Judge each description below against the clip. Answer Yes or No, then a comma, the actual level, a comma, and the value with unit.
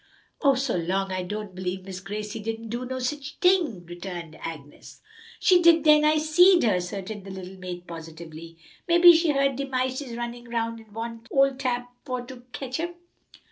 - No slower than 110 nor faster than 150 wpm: No, average, 180 wpm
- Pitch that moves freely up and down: Yes, wide, 6.8 semitones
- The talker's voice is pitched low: No, high, 230 Hz